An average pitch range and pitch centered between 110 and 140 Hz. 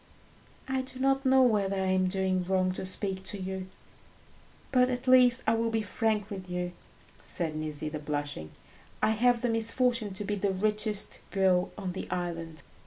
No: average, 3.8 semitones; high, 195 Hz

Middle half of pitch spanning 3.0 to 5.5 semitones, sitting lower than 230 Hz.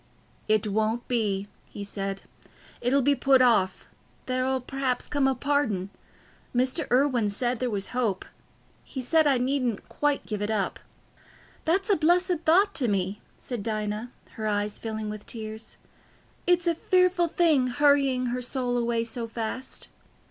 No: average, 4.7 semitones; high, 245 Hz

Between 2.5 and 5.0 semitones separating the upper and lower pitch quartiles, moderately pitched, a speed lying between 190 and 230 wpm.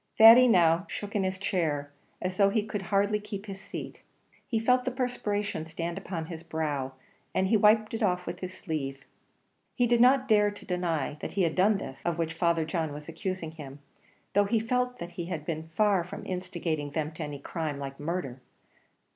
Yes: average, 4.6 semitones; medium, 180 Hz; average, 200 wpm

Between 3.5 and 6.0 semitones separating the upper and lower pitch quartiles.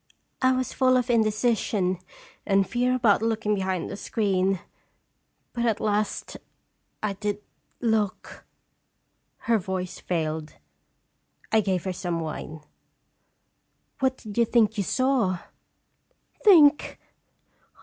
Yes: average, 4.0 semitones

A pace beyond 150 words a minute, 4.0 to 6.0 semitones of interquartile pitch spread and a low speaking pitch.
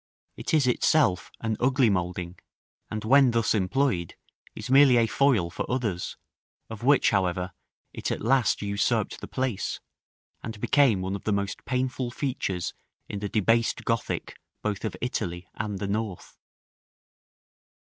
No: average, 145 wpm; average, 4.8 semitones; low, 110 Hz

